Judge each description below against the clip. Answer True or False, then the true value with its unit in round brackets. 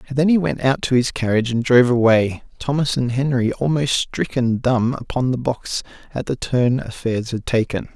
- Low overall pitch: True (125 Hz)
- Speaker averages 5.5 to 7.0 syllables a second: False (5.1 syllables/s)